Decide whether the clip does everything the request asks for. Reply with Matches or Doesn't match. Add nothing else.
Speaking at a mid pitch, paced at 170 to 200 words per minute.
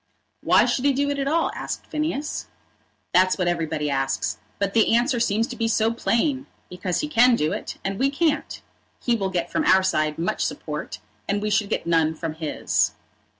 Doesn't match